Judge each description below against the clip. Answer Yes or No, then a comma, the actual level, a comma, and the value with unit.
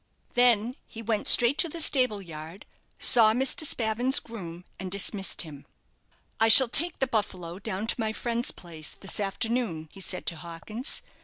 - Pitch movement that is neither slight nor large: Yes, average, 5.0 semitones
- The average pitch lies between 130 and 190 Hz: No, high, 215 Hz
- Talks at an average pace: Yes, average, 165 wpm